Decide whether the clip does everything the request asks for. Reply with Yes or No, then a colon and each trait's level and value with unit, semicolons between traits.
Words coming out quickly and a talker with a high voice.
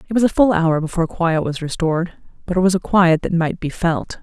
No: fast, 255 wpm; medium, 175 Hz